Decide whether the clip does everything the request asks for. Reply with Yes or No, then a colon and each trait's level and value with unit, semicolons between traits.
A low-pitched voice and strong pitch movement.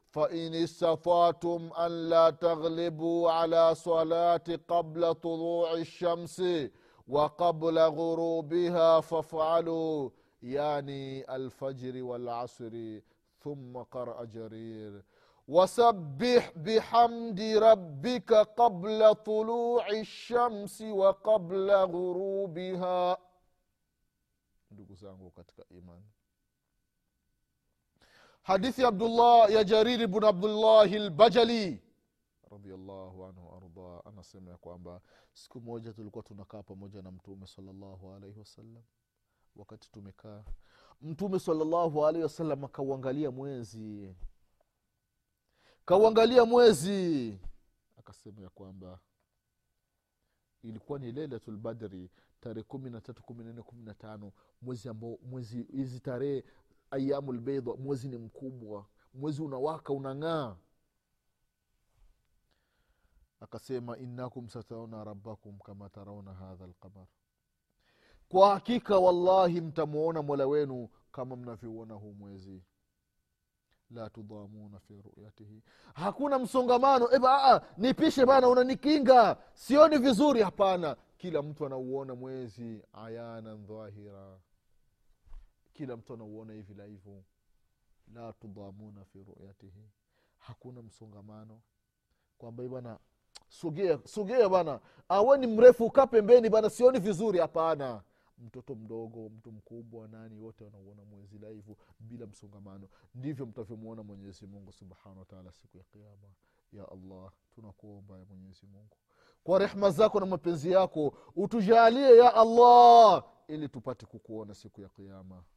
Yes: low, 125 Hz; wide, 8.8 semitones